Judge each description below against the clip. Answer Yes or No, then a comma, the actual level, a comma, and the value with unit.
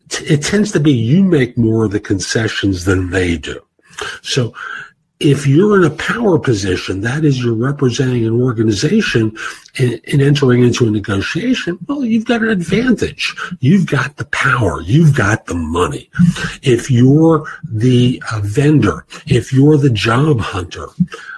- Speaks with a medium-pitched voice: No, low, 130 Hz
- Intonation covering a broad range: Yes, wide, 6.1 semitones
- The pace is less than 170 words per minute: Yes, average, 150 wpm